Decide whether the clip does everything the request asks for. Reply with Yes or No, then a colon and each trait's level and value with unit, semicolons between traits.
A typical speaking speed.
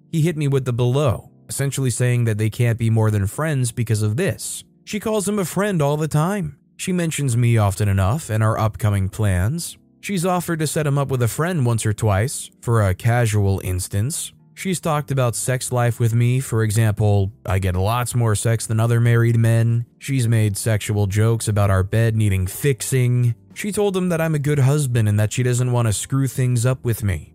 No: fast, 215 wpm